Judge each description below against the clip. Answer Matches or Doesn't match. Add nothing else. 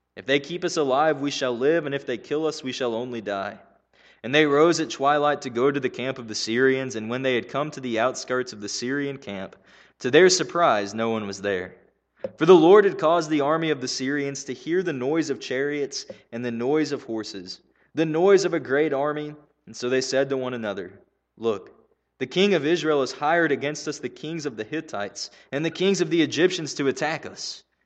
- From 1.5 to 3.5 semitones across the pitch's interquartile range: Doesn't match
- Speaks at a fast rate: Matches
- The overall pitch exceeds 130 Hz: Matches